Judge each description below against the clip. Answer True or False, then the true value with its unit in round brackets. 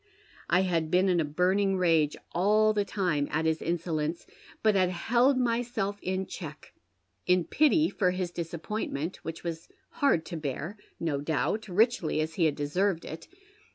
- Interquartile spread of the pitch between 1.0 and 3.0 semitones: False (4.1 semitones)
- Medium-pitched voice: True (180 Hz)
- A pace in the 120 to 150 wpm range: False (160 wpm)